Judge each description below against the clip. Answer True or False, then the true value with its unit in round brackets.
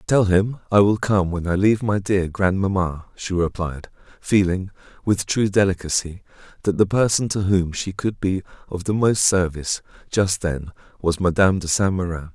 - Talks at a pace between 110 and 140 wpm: False (175 wpm)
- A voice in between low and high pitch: False (95 Hz)